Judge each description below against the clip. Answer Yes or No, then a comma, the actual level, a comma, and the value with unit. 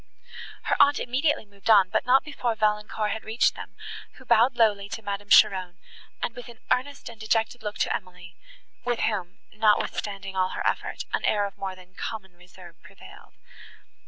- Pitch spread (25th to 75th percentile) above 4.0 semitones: No, average, 3.4 semitones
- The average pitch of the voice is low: No, high, 210 Hz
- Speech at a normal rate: Yes, average, 175 wpm